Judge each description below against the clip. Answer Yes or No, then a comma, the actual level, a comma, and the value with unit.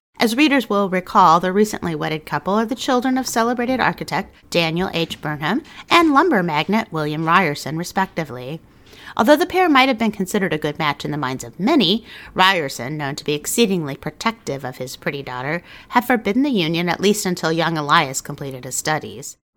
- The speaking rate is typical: Yes, average, 185 wpm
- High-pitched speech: No, medium, 175 Hz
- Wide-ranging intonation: Yes, wide, 7.2 semitones